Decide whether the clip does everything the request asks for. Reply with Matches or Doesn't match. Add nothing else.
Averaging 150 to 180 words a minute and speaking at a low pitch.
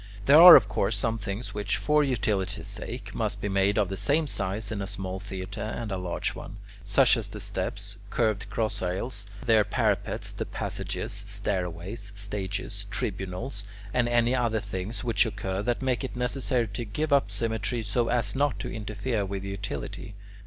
Matches